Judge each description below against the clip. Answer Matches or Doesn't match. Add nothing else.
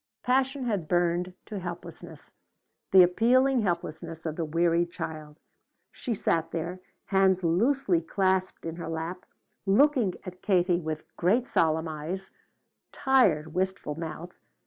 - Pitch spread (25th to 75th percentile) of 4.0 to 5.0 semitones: Doesn't match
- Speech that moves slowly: Matches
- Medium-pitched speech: Matches